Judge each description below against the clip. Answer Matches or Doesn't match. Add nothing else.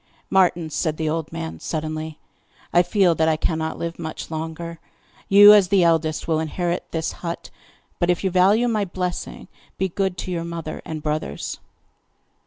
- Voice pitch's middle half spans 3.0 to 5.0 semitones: Doesn't match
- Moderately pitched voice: Matches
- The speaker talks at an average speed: Matches